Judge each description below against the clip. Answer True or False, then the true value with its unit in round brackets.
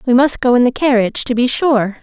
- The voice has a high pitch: True (245 Hz)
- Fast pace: True (265 wpm)